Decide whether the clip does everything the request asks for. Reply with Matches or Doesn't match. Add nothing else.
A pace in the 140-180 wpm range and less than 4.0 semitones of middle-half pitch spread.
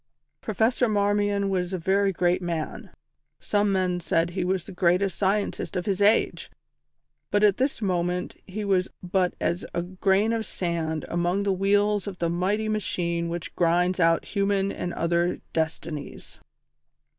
Matches